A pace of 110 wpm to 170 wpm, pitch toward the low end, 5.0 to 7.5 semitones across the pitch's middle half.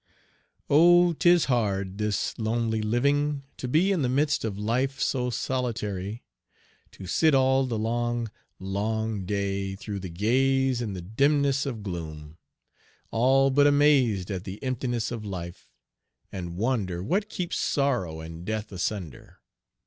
Yes: average, 140 wpm; low, 115 Hz; wide, 5.5 semitones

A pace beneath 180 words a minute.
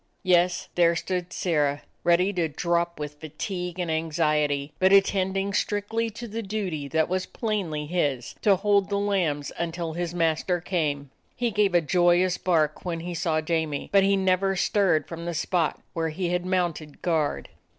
Yes: average, 170 wpm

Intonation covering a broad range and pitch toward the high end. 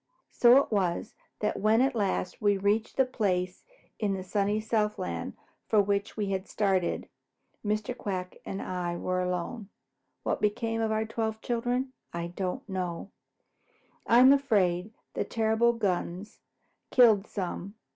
No: average, 3.4 semitones; high, 205 Hz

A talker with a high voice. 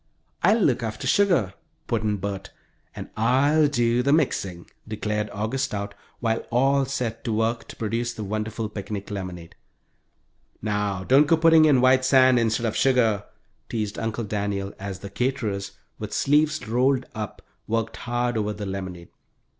No: low, 115 Hz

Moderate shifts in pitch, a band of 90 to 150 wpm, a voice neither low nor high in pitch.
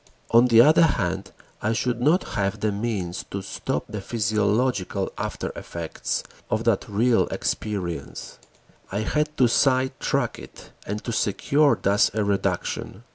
No: average, 3.7 semitones; average, 140 wpm; low, 110 Hz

